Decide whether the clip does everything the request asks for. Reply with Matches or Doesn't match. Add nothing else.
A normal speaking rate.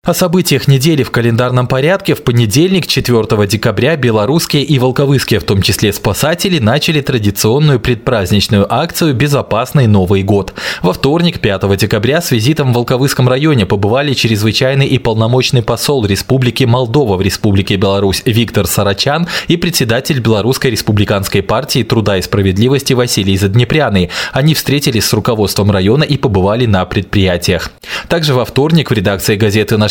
Matches